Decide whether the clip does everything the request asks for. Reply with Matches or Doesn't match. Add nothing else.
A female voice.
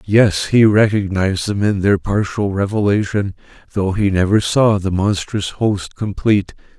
Doesn't match